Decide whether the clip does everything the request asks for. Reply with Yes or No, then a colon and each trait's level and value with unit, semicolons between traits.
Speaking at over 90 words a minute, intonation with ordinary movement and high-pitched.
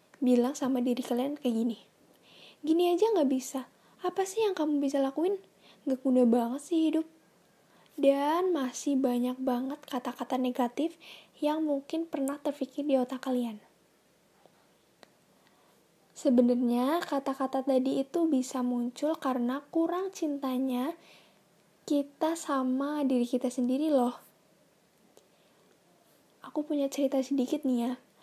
Yes: average, 115 wpm; average, 3.1 semitones; very high, 270 Hz